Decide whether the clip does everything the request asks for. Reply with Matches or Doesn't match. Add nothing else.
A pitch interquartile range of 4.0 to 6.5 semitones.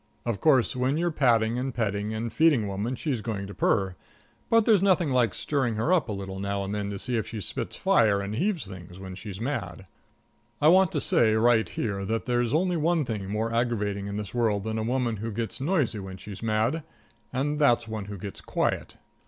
Matches